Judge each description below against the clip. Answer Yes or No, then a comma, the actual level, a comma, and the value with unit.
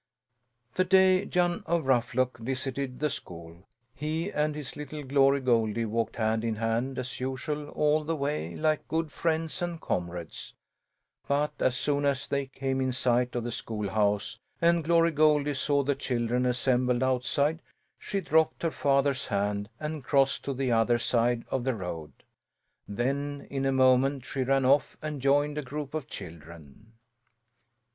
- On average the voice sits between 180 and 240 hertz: No, low, 135 Hz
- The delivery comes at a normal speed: Yes, average, 160 wpm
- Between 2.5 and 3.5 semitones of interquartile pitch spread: No, average, 4.0 semitones